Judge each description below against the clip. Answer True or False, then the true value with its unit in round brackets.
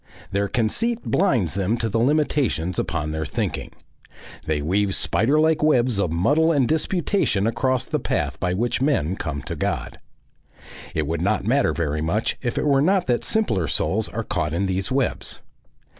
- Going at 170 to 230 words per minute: True (175 wpm)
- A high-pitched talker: False (110 Hz)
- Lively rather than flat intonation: True (8.4 semitones)